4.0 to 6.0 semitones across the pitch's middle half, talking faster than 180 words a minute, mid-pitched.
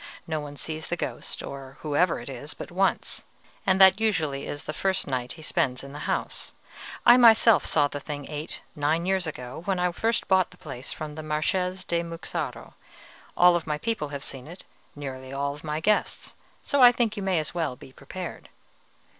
Yes: average, 4.5 semitones; average, 190 wpm; medium, 155 Hz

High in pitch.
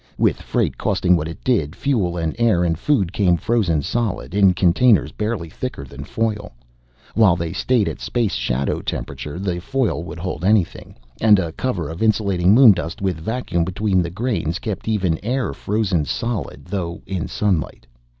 No: very low, 95 Hz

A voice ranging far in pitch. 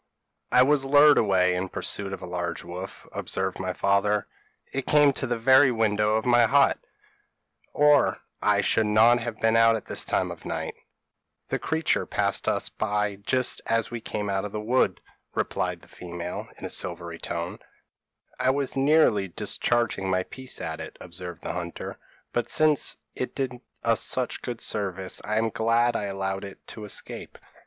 No: average, 4.6 semitones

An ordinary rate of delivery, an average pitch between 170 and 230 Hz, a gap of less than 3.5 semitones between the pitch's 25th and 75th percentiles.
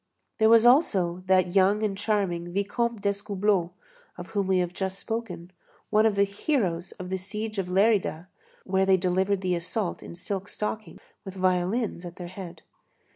Yes: average, 170 wpm; high, 190 Hz; average, 2.7 semitones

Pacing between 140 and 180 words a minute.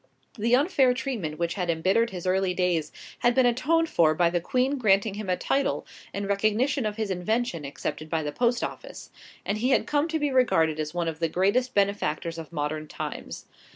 No: average, 200 wpm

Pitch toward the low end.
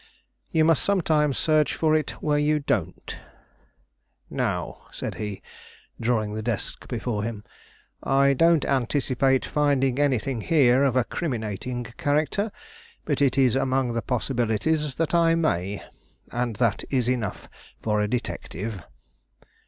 Yes: low, 130 Hz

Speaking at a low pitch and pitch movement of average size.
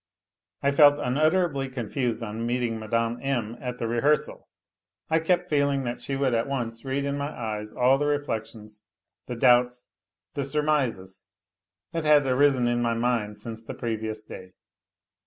Yes: low, 125 Hz; average, 3.6 semitones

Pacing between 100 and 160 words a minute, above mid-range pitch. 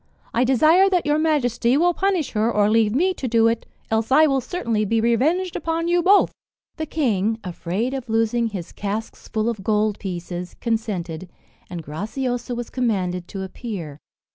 No: average, 170 wpm; high, 230 Hz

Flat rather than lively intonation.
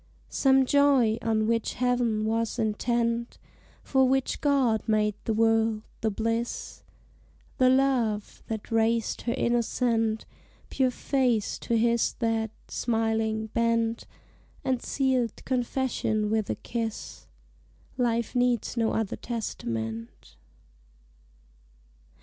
Yes: narrow, 2.1 semitones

